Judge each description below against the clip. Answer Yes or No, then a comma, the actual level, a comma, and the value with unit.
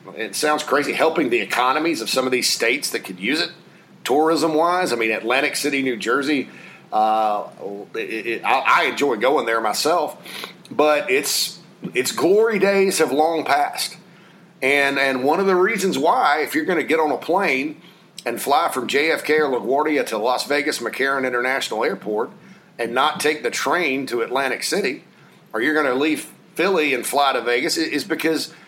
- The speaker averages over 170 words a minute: Yes, average, 185 wpm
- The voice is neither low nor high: Yes, medium, 150 Hz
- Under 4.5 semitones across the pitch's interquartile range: No, wide, 5.4 semitones